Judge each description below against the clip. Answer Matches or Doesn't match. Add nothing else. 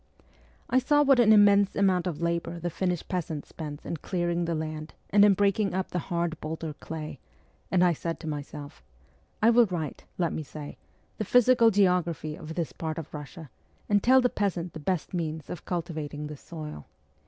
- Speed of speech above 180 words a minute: Matches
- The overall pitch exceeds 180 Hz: Doesn't match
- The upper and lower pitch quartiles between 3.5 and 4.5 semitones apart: Matches